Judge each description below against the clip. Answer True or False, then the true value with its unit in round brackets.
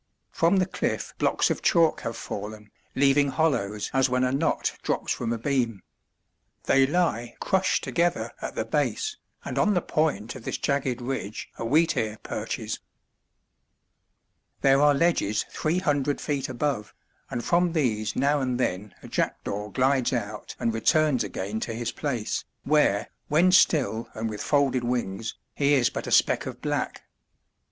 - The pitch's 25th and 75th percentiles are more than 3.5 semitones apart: True (4.9 semitones)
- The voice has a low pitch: True (130 Hz)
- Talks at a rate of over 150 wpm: True (160 wpm)